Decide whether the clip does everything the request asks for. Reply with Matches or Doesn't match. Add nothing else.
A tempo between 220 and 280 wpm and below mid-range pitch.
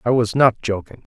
Doesn't match